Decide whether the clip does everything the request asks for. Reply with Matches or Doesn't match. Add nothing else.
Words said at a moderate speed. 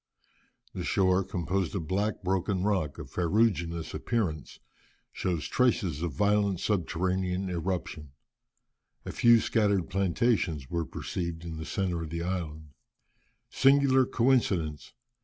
Doesn't match